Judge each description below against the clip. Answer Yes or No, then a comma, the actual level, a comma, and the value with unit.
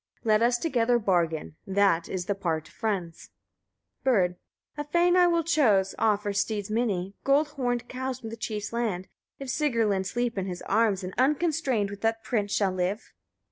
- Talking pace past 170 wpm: Yes, average, 180 wpm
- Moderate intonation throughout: Yes, average, 4.7 semitones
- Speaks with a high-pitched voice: Yes, high, 220 Hz